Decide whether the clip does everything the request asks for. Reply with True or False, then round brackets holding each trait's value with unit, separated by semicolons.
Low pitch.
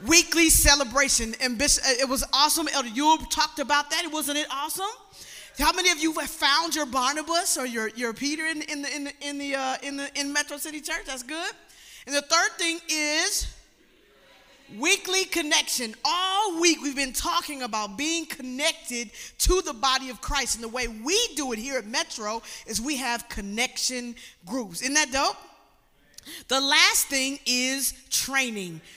False (285 Hz)